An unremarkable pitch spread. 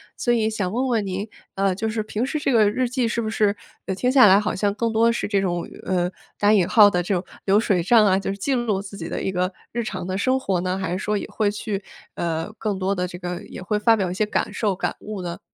Yes: average, 3.0 semitones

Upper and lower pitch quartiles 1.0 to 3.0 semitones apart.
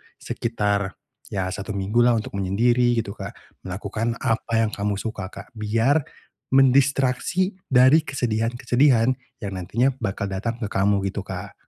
No: average, 3.7 semitones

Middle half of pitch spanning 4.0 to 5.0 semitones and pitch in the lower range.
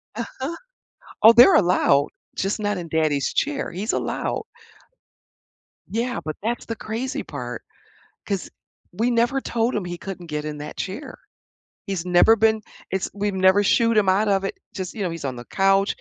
No: average, 4.5 semitones; high, 195 Hz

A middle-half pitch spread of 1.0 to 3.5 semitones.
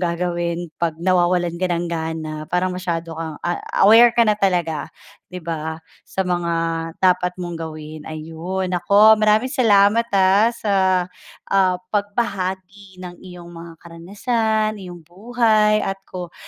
Yes: average, 3.0 semitones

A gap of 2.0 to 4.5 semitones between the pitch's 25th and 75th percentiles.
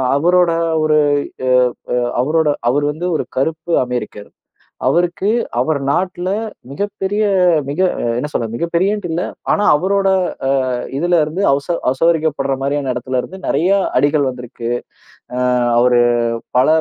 No: average, 5.0 semitones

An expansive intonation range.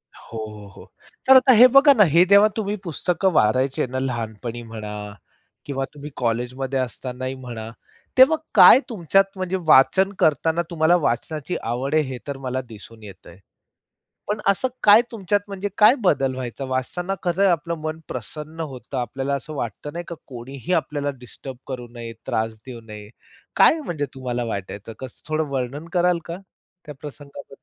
Yes: wide, 6.0 semitones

